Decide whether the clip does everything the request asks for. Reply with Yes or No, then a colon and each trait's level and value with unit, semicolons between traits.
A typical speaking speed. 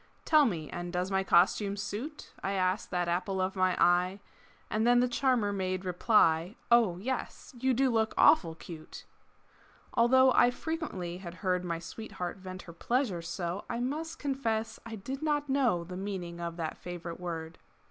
Yes: average, 170 wpm